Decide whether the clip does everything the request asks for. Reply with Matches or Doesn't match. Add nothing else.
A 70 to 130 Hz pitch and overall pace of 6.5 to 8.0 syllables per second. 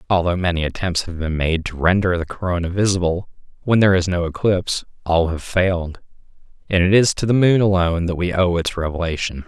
Doesn't match